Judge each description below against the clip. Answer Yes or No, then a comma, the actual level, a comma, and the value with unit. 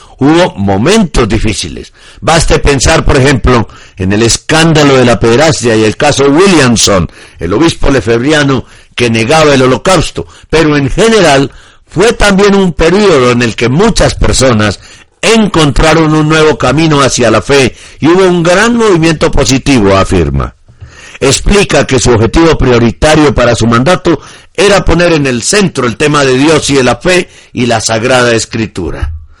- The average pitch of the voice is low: Yes, low, 130 Hz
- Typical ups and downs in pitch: No, wide, 5.9 semitones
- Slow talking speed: No, average, 155 wpm